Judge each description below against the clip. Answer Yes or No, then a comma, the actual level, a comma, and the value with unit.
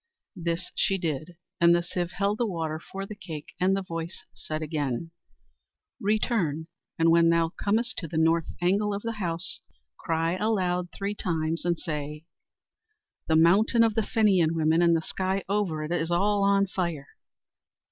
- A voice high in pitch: No, medium, 175 Hz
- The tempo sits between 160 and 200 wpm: Yes, average, 165 wpm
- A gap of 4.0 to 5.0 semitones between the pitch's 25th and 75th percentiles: No, average, 3.4 semitones